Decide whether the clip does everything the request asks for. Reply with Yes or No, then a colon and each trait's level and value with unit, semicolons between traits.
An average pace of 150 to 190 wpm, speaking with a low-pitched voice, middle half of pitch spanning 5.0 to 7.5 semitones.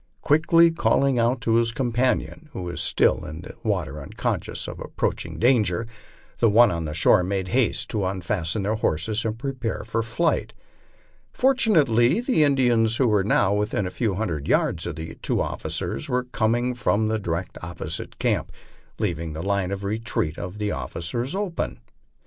Yes: average, 170 wpm; low, 110 Hz; average, 5.3 semitones